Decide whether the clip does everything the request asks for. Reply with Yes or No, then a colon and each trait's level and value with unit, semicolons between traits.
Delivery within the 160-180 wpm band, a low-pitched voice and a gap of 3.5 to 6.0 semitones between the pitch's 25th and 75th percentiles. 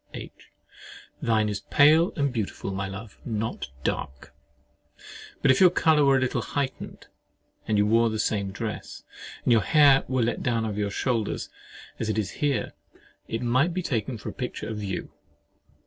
Yes: average, 175 wpm; low, 115 Hz; average, 4.3 semitones